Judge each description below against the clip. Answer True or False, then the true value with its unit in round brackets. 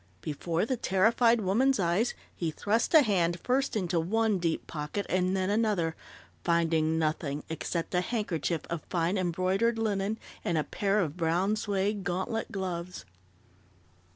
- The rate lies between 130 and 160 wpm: True (145 wpm)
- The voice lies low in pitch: False (185 Hz)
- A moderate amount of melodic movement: True (3.9 semitones)